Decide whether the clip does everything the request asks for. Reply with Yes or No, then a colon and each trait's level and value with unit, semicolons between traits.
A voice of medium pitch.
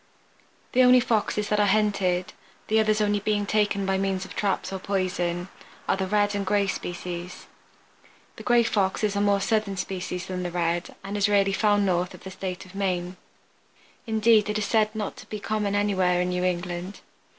No: high, 200 Hz